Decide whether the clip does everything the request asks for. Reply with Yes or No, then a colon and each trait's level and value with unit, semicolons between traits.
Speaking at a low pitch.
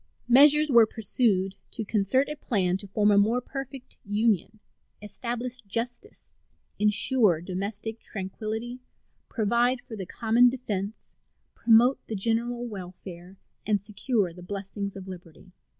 No: high, 215 Hz